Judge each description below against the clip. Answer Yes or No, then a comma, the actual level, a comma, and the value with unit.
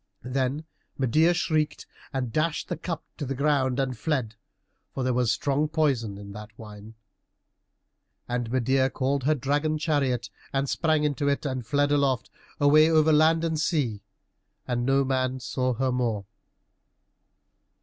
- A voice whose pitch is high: No, low, 135 Hz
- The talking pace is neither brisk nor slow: Yes, average, 150 wpm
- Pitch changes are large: No, average, 3.4 semitones